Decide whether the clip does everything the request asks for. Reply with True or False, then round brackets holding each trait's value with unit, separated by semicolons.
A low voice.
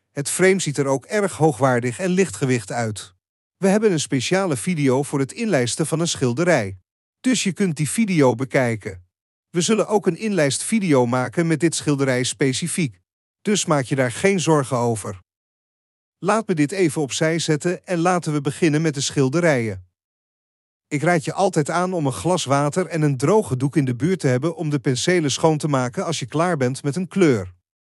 False (150 Hz)